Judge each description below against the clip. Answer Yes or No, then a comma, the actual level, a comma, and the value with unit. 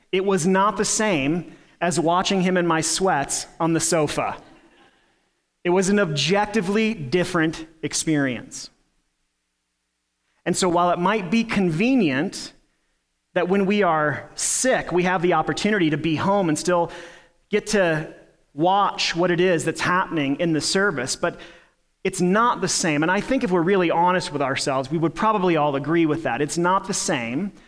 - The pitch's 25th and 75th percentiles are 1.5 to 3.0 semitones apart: No, average, 3.6 semitones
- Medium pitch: Yes, medium, 175 Hz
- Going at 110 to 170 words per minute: Yes, average, 165 wpm